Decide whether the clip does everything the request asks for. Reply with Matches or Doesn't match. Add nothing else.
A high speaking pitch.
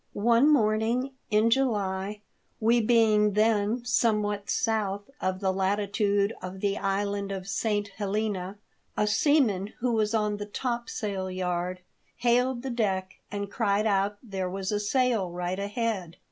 Matches